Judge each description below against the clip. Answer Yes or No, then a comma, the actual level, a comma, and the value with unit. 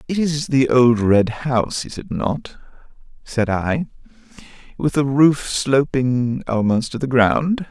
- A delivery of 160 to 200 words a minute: No, average, 150 wpm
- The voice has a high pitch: No, low, 130 Hz